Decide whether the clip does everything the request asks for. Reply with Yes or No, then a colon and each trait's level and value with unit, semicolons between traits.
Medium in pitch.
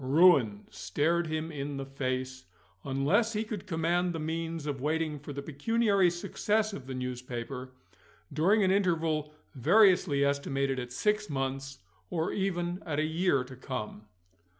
Yes: medium, 155 Hz